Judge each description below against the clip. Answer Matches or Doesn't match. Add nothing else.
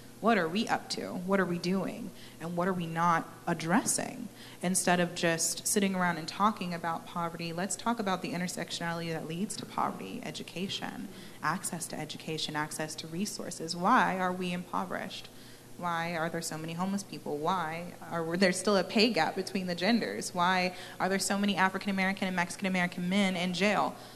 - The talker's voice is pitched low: Doesn't match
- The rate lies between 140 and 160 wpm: Doesn't match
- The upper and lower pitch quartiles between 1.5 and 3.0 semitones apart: Matches